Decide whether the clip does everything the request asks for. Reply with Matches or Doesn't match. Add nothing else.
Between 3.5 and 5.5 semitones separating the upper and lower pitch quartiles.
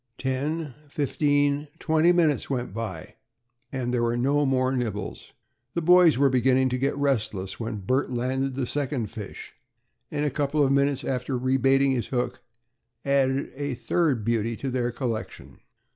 Doesn't match